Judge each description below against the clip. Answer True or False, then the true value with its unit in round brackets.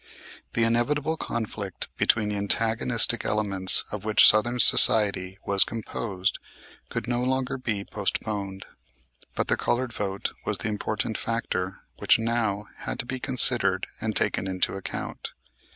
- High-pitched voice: False (110 Hz)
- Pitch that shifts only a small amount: False (3.1 semitones)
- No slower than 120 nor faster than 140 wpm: True (135 wpm)